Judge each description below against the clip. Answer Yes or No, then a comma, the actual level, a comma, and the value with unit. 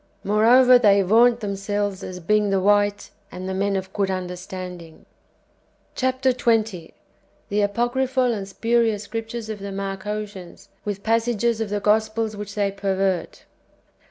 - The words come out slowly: No, average, 150 wpm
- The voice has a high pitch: Yes, high, 205 Hz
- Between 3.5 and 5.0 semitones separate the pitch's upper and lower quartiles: No, average, 2.7 semitones